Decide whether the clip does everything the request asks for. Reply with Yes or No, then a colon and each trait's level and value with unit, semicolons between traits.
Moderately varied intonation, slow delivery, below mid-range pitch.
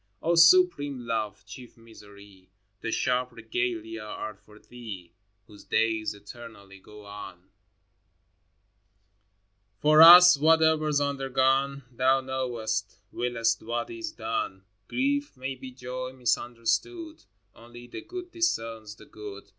Yes: average, 4.1 semitones; slow, 115 wpm; low, 120 Hz